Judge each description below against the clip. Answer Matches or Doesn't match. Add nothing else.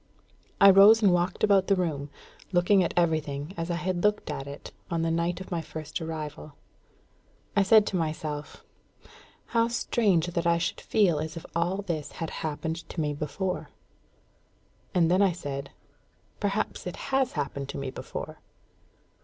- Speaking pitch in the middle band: Matches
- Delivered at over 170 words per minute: Doesn't match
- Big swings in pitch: Doesn't match